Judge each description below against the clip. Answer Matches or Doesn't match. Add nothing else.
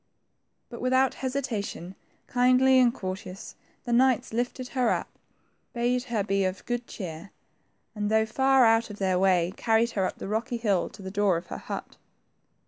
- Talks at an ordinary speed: Matches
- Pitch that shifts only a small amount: Doesn't match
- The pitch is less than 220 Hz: Doesn't match